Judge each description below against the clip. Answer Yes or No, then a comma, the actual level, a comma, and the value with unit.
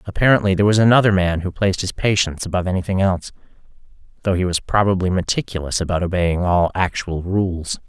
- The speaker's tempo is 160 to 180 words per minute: Yes, average, 170 wpm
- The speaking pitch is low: Yes, very low, 95 Hz